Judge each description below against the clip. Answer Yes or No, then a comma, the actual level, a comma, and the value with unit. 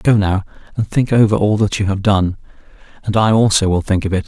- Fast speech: Yes, fast, 240 wpm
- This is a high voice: No, low, 100 Hz